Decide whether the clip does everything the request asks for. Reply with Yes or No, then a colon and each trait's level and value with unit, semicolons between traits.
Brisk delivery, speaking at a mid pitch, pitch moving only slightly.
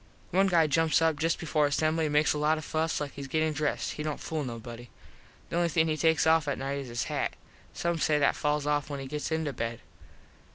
Yes: fast, 240 wpm; medium, 150 Hz; narrow, 2.0 semitones